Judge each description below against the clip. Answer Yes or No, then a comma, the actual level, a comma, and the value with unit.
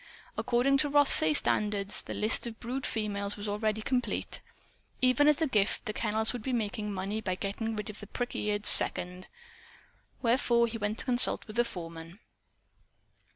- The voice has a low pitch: No, high, 215 Hz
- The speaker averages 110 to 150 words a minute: No, average, 170 wpm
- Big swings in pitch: No, average, 3.0 semitones